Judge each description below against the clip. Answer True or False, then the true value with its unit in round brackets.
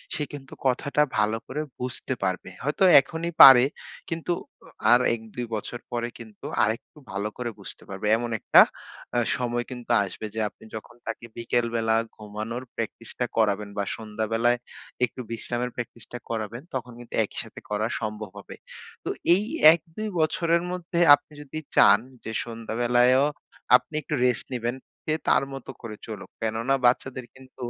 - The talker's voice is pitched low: True (120 Hz)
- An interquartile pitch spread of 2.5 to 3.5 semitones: True (2.8 semitones)